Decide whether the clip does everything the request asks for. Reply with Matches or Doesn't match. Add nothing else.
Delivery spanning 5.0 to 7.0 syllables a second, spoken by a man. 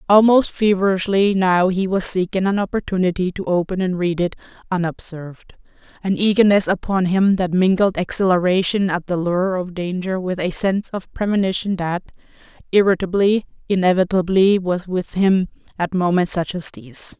Doesn't match